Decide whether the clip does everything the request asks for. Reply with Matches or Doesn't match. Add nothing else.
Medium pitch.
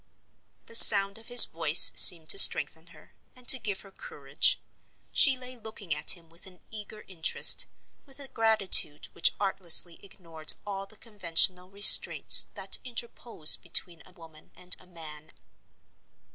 Doesn't match